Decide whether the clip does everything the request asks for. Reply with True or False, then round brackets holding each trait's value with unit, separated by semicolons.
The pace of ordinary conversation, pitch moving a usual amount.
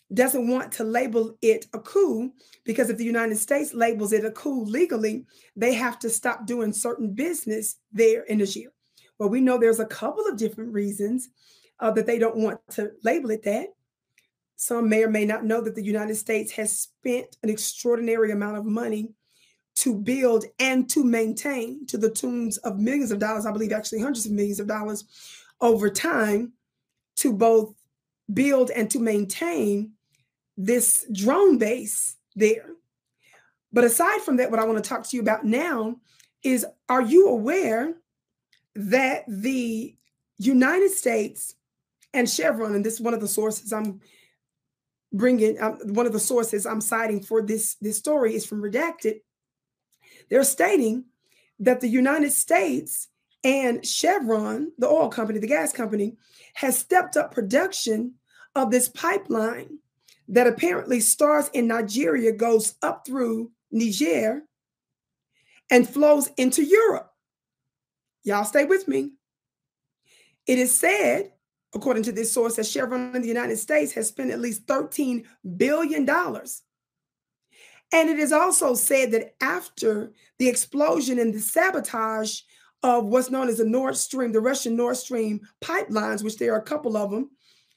True (155 wpm; 3.3 semitones)